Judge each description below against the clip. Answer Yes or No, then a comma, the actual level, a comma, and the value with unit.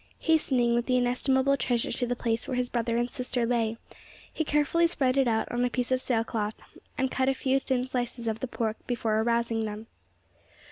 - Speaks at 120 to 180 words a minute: No, average, 200 wpm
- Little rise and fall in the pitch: Yes, narrow, 2.1 semitones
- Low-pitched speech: No, high, 245 Hz